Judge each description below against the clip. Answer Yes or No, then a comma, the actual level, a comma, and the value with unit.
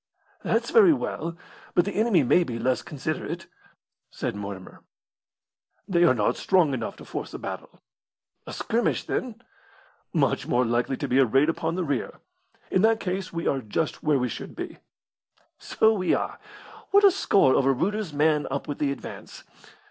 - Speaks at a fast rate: No, average, 170 wpm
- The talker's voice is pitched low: No, medium, 160 Hz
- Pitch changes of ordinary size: No, wide, 6.7 semitones